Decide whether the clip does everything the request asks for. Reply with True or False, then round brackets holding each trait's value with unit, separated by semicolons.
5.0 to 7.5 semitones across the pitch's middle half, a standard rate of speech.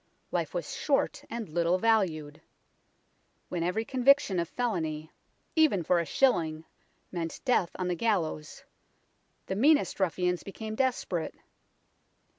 False (5.4 semitones; 120 wpm)